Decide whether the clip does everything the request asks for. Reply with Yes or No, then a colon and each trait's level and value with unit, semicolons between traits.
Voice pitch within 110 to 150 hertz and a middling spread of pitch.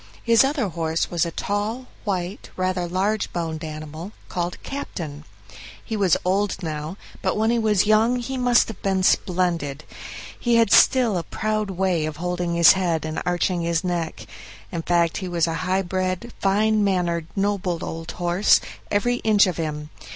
No: medium, 185 Hz; average, 3.7 semitones